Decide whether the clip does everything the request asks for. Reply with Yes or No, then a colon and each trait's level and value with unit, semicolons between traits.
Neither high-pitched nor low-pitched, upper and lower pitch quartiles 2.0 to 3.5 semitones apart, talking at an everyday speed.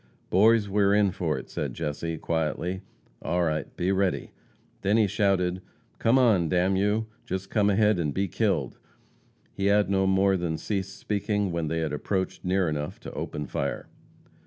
No: very low, 95 Hz; average, 2.9 semitones; average, 180 wpm